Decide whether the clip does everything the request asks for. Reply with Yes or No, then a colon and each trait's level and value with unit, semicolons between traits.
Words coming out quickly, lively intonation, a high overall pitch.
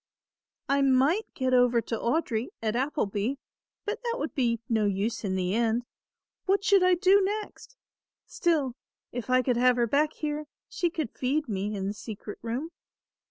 No: average, 170 wpm; wide, 5.8 semitones; very high, 255 Hz